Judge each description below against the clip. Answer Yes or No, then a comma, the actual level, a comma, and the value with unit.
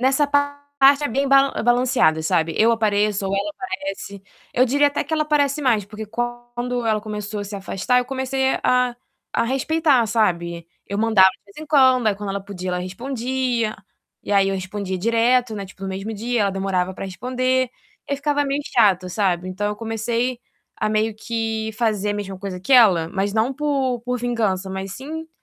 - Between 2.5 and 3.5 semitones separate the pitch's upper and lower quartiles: No, average, 4.6 semitones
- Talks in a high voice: Yes, high, 225 Hz